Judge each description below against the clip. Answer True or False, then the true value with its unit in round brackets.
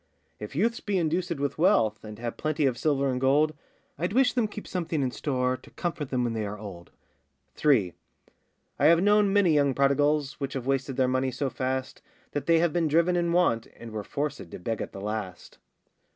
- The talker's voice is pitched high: False (140 Hz)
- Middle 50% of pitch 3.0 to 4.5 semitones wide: False (5.3 semitones)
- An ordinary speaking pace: False (210 wpm)